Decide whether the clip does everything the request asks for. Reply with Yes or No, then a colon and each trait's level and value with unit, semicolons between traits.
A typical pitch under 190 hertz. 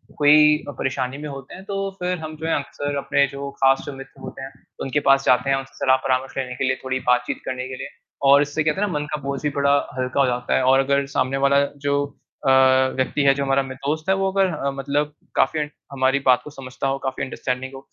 Yes: low, 135 Hz